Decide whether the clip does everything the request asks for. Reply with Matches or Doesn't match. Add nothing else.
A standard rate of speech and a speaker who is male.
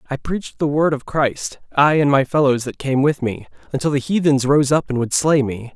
Doesn't match